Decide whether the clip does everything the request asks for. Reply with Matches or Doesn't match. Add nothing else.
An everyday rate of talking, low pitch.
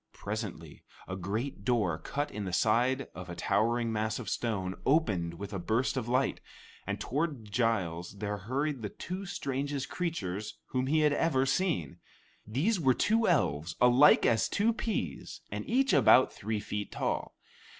Matches